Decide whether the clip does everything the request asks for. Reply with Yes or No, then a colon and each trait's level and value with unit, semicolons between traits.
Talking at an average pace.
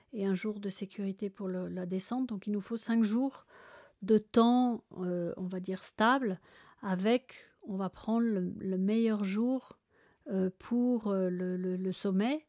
Yes: average, 175 wpm